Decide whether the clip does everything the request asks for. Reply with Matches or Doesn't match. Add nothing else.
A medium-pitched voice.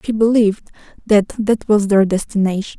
Doesn't match